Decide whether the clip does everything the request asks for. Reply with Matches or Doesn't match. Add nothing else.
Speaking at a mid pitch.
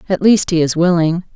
Matches